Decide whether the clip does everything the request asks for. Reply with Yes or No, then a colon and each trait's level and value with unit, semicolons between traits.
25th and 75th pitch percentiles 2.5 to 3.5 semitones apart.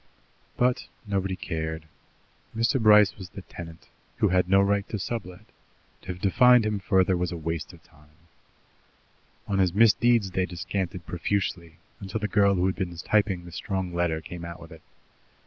Yes: average, 2.8 semitones